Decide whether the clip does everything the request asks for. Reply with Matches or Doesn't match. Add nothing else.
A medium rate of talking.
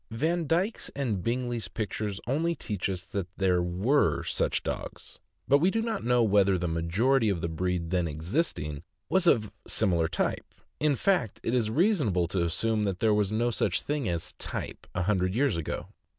Matches